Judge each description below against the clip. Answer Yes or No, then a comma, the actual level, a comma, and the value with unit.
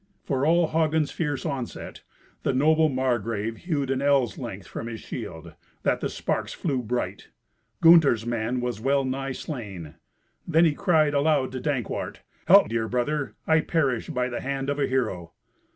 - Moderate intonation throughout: Yes, average, 4.0 semitones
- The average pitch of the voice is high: No, low, 135 Hz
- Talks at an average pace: Yes, average, 165 wpm